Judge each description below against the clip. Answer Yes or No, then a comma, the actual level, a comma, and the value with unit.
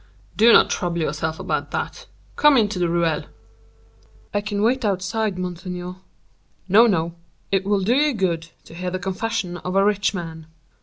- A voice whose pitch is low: No, medium, 185 Hz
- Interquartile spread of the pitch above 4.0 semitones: No, average, 3.3 semitones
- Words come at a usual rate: Yes, average, 165 wpm